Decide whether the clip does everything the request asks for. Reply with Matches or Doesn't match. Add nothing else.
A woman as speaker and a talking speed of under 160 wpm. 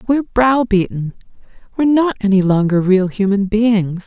Matches